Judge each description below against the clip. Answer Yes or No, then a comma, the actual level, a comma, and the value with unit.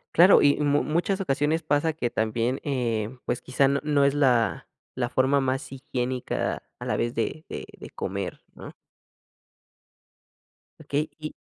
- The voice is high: No, low, 135 Hz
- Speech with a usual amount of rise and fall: Yes, average, 3.3 semitones